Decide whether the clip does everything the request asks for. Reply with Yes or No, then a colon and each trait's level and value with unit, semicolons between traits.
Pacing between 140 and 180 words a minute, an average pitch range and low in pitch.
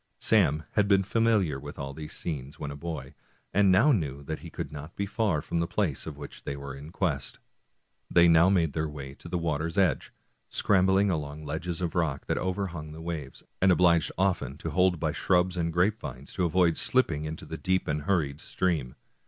No: fast, 205 wpm; average, 3.9 semitones; very low, 85 Hz